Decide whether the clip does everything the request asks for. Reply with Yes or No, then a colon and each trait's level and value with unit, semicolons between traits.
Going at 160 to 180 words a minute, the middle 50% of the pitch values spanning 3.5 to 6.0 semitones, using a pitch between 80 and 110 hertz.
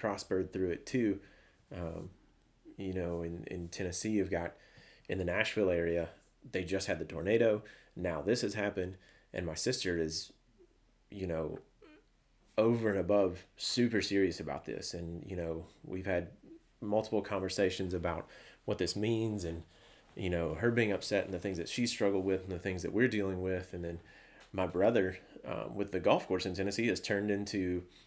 No: average, 175 wpm; average, 2.9 semitones; very low, 95 Hz